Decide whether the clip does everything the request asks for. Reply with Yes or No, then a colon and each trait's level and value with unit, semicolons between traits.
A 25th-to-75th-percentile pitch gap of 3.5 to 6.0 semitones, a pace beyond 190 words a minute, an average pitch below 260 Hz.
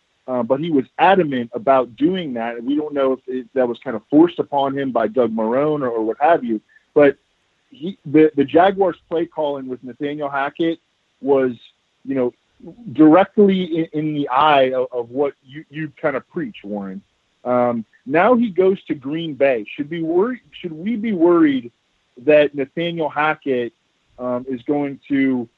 No: average, 4.6 semitones; average, 180 wpm; medium, 140 Hz